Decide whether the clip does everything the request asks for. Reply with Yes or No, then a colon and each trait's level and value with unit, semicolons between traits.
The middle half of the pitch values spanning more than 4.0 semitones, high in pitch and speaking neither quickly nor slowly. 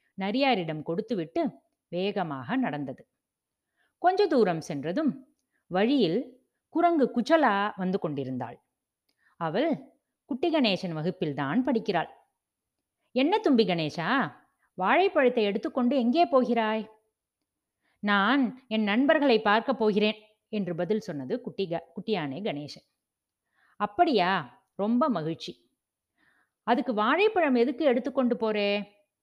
Yes: wide, 5.6 semitones; high, 220 Hz; average, 90 wpm